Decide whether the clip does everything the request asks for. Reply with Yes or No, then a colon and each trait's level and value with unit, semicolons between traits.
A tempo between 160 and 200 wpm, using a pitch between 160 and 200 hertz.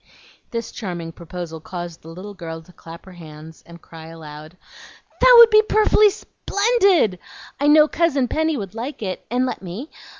Yes: average, 170 wpm; high, 190 Hz